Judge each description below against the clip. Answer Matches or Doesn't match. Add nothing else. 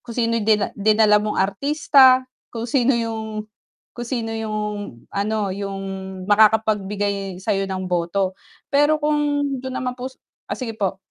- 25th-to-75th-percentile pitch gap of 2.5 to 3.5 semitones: Doesn't match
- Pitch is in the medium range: Doesn't match